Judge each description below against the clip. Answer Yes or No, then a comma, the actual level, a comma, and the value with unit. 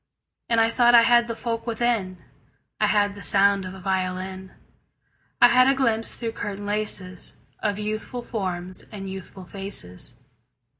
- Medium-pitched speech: No, high, 205 Hz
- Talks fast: No, average, 155 wpm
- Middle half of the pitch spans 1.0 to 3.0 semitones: No, average, 3.4 semitones